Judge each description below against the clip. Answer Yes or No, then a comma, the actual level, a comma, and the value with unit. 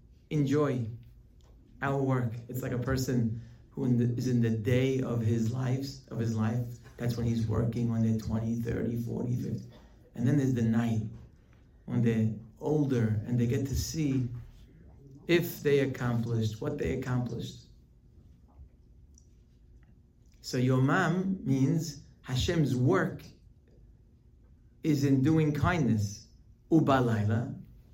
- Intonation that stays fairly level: No, average, 3.0 semitones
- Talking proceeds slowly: Yes, slow, 130 wpm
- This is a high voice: No, low, 120 Hz